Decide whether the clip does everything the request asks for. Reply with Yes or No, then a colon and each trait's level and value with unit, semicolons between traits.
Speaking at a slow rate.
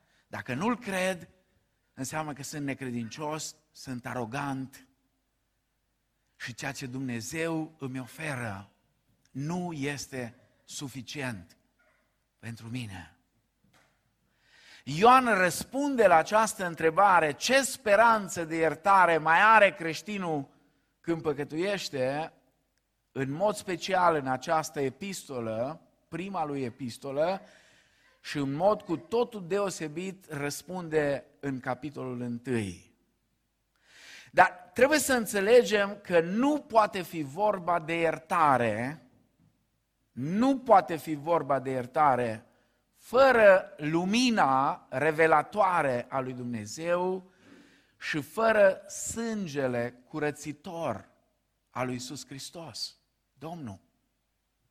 Yes: slow, 95 wpm